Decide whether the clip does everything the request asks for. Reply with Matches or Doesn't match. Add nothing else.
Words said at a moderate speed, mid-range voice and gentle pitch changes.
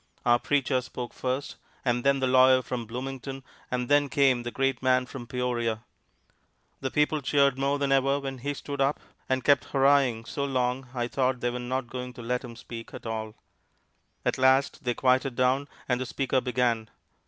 Doesn't match